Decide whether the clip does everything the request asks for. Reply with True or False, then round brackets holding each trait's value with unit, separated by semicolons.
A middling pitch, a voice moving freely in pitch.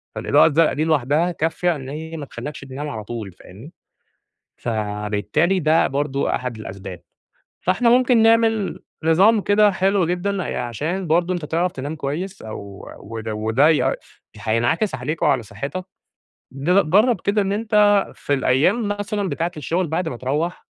True (160 Hz; 6.8 semitones)